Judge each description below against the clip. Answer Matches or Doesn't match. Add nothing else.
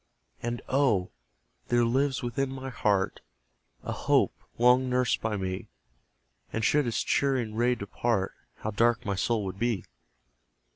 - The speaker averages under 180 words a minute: Matches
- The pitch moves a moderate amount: Matches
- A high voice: Doesn't match